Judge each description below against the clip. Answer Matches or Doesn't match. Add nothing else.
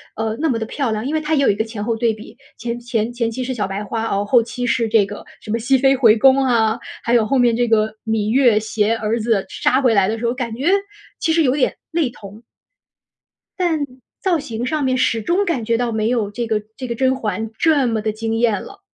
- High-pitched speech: Matches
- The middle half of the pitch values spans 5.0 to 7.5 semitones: Doesn't match